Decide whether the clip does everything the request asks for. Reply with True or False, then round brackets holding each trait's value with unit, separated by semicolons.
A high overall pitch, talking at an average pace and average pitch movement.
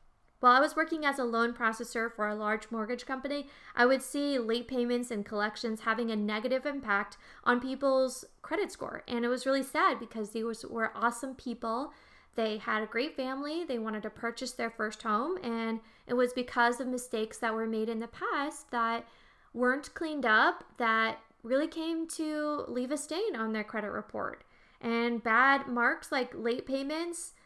True (245 Hz; 180 wpm; 3.7 semitones)